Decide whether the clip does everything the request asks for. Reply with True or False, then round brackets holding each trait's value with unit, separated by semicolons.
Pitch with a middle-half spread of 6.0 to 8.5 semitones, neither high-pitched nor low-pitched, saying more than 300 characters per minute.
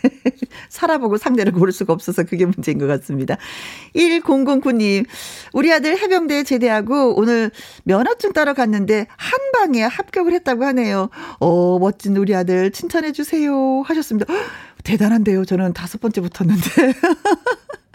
False (8.0 semitones; 250 Hz; 310 characters per minute)